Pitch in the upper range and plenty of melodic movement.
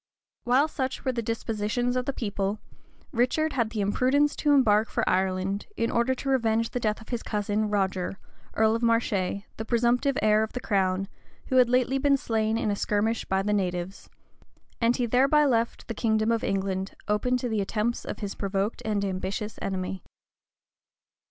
No: high, 220 Hz; average, 3.6 semitones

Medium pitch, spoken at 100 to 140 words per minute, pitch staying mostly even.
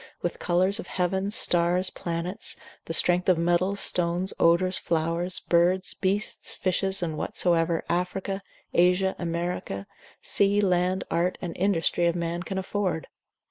Yes: medium, 180 Hz; slow, 135 wpm; narrow, 1.8 semitones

